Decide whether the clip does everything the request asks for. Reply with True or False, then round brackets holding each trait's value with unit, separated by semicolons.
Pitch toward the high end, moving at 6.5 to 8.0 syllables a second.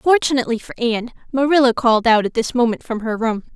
True (240 Hz; 6.6 syllables/s)